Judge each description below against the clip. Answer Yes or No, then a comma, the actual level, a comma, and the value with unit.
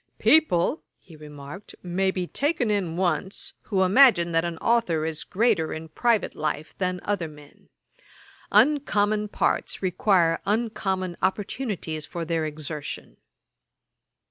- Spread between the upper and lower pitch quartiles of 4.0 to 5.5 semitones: Yes, average, 4.5 semitones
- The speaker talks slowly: Yes, slow, 120 wpm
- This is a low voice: No, medium, 185 Hz